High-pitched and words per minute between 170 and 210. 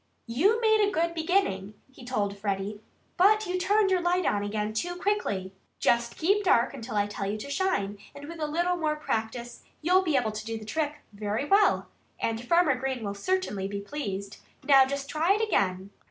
Yes: very high, 270 Hz; average, 195 wpm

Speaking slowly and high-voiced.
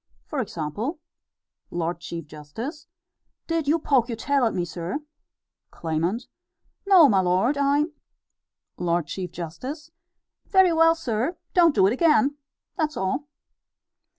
Yes: slow, 125 wpm; high, 240 Hz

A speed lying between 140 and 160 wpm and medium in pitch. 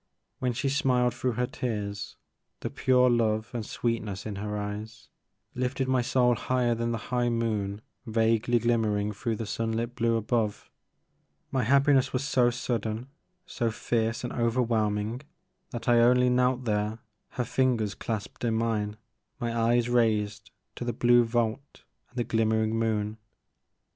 No: average, 150 wpm; low, 115 Hz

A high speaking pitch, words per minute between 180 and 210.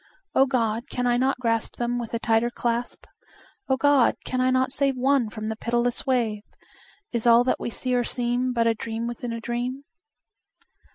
Yes: high, 240 Hz; average, 190 wpm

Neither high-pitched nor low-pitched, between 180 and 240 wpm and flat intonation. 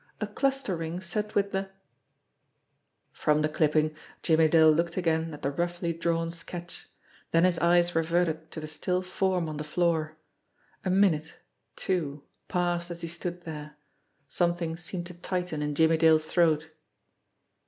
No: medium, 170 Hz; average, 155 wpm; narrow, 2.0 semitones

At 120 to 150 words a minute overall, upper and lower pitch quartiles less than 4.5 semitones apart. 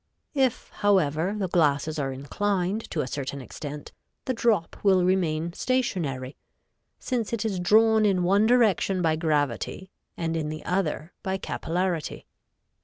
No: average, 140 wpm; average, 4.9 semitones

